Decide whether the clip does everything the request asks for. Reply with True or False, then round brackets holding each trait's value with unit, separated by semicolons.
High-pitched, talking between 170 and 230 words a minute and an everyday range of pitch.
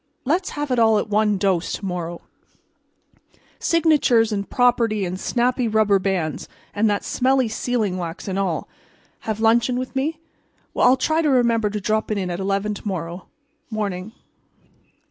False (215 Hz; 155 wpm; 4.2 semitones)